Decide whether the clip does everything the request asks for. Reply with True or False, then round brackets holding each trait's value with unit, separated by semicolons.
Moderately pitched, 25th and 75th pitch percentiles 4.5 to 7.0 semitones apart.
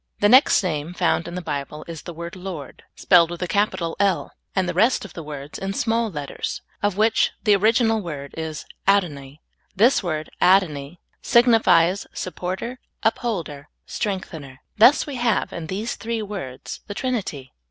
True (180 Hz; 5.4 semitones)